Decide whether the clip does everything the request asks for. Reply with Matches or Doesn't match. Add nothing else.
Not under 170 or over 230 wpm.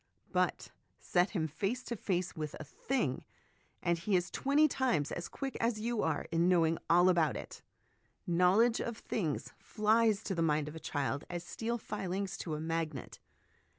Matches